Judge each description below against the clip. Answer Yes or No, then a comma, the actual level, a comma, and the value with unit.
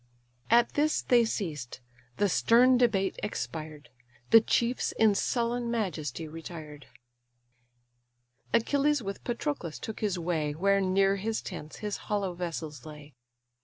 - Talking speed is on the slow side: Yes, slow, 125 wpm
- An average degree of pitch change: No, wide, 6.5 semitones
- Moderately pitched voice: No, high, 195 Hz